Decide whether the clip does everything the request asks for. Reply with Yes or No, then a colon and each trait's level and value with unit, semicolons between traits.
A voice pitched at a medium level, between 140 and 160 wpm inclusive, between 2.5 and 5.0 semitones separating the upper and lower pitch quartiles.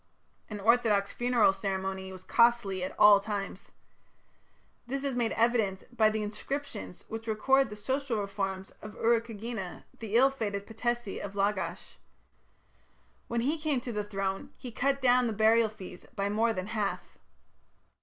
No: high, 220 Hz; average, 155 wpm; average, 3.3 semitones